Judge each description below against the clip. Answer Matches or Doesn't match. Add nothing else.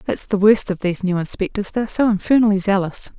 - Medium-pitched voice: Doesn't match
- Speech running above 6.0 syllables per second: Matches